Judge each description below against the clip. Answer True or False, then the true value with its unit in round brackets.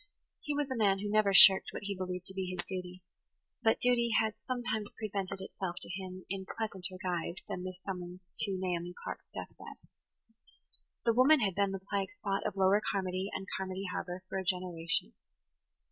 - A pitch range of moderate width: False (1.9 semitones)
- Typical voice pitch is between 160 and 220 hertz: True (190 Hz)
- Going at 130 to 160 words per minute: False (185 wpm)